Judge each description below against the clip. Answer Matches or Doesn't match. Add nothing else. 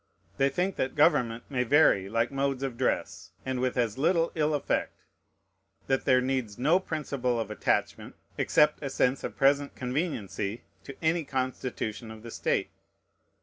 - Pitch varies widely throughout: Doesn't match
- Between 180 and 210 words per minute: Doesn't match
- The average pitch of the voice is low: Matches